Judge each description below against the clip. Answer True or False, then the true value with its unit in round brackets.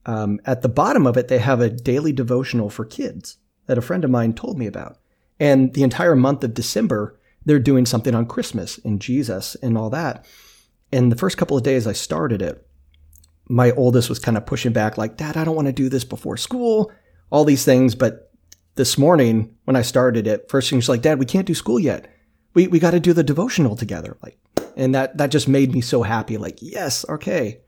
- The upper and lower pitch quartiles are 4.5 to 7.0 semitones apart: False (3.9 semitones)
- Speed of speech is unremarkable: False (225 wpm)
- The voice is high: False (125 Hz)